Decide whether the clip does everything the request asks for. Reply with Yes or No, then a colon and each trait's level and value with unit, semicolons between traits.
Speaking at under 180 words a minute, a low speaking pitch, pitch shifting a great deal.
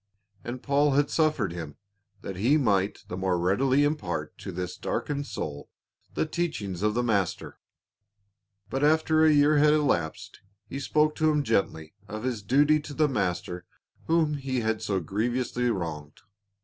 Yes: average, 160 wpm; low, 120 Hz; wide, 7.6 semitones